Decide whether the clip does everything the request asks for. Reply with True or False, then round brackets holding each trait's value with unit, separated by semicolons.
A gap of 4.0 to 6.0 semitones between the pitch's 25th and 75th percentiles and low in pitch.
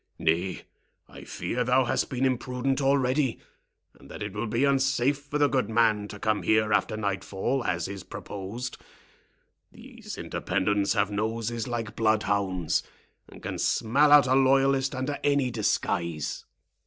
True (4.5 semitones; 115 Hz)